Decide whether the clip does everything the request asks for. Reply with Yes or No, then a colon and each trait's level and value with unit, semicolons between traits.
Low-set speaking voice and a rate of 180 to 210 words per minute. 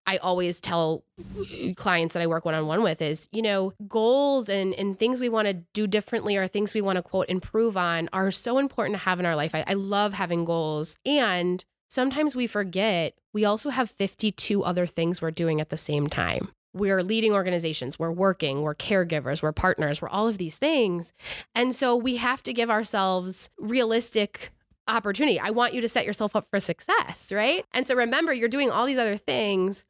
No: high, 195 Hz; average, 200 wpm